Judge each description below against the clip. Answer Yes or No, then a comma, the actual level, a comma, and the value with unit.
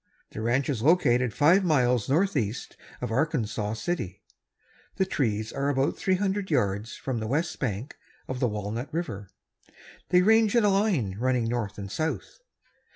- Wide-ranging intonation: Yes, wide, 7.6 semitones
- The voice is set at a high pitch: No, low, 130 Hz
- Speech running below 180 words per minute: Yes, average, 155 wpm